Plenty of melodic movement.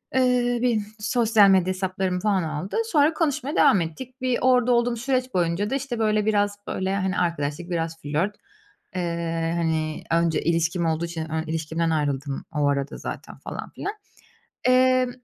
Yes: wide, 6.8 semitones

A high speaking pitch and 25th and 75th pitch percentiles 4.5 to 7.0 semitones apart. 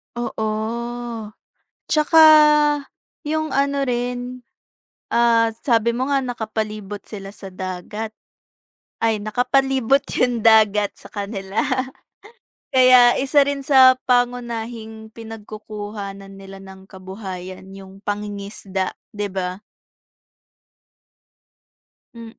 No: high, 220 Hz; average, 3.8 semitones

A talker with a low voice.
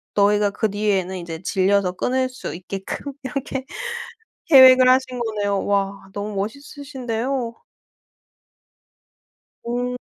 No: high, 220 Hz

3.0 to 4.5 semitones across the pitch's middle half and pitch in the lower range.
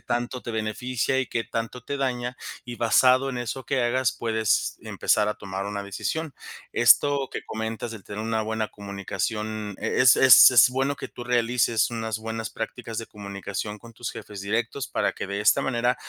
No: narrow, 2.5 semitones; low, 115 Hz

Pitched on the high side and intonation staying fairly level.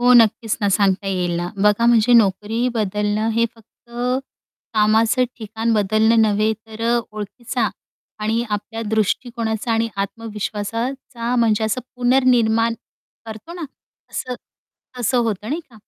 Yes: high, 225 Hz; narrow, 2.0 semitones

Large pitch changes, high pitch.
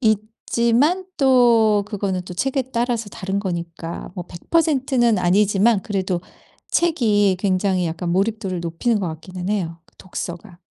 No: average, 4.5 semitones; high, 205 Hz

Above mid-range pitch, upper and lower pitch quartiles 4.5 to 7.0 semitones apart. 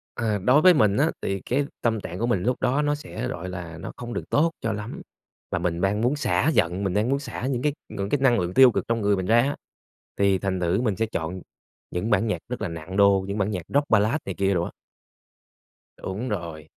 No: low, 105 Hz; average, 4.8 semitones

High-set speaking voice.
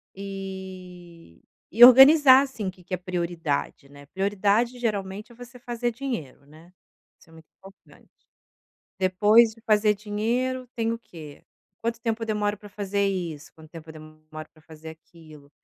Yes: high, 195 Hz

